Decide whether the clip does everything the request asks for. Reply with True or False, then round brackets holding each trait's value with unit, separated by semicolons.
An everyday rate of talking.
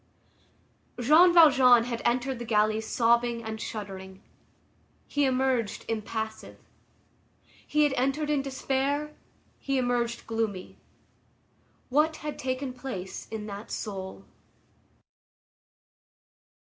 False (95 wpm)